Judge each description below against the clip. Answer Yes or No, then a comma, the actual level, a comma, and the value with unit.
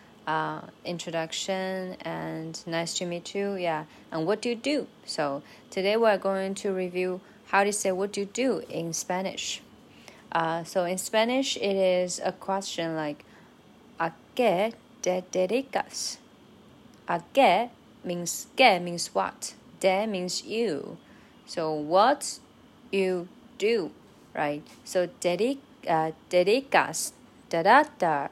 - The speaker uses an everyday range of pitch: Yes, average, 3.9 semitones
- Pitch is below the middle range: No, medium, 185 Hz